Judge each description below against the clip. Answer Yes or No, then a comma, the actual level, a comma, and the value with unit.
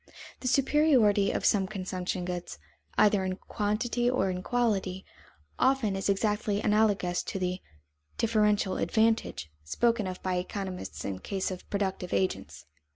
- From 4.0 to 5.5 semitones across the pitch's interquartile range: No, average, 3.1 semitones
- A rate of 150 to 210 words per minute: No, slow, 135 wpm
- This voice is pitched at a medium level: No, high, 200 Hz